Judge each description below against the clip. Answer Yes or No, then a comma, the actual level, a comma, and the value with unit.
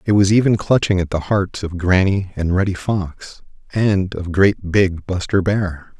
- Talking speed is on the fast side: No, average, 180 wpm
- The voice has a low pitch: Yes, very low, 95 Hz